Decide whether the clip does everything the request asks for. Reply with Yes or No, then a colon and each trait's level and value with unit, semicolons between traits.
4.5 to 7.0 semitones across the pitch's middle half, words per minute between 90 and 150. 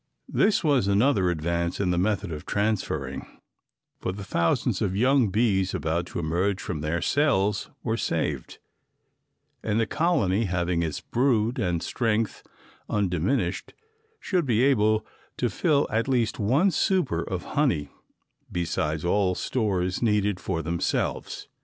Yes: average, 5.2 semitones; slow, 135 wpm